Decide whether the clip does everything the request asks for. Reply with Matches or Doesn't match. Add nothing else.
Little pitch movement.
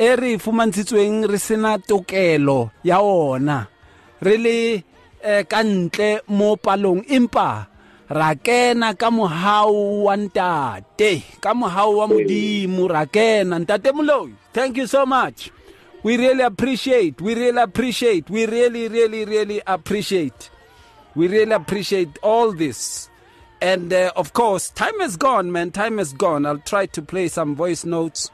Doesn't match